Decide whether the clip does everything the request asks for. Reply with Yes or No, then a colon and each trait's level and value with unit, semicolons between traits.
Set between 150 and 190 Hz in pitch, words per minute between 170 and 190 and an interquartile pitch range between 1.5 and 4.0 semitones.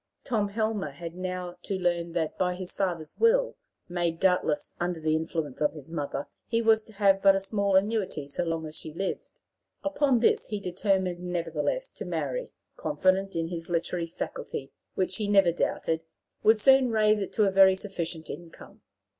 Yes: medium, 185 Hz; average, 180 wpm; average, 3.7 semitones